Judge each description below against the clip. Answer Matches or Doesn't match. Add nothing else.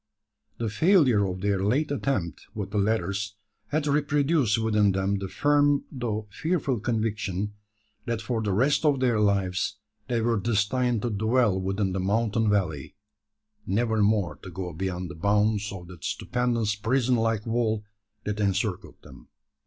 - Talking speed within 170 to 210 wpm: Doesn't match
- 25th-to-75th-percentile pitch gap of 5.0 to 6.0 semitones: Doesn't match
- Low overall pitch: Matches